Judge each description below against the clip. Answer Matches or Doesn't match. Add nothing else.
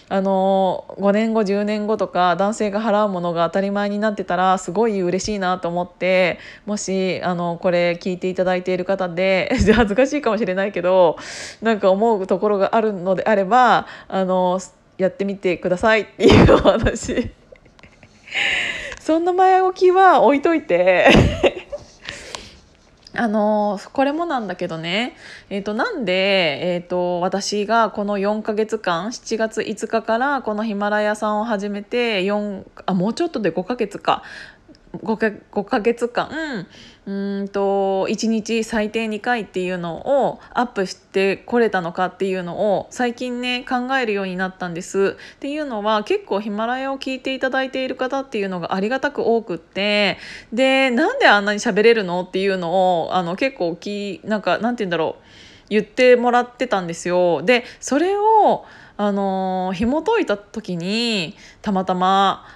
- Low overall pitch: Doesn't match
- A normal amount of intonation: Matches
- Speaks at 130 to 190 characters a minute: Doesn't match